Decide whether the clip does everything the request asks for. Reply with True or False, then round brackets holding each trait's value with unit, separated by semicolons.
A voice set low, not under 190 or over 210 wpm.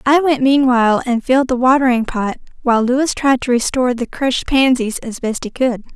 False (250 Hz; 200 wpm)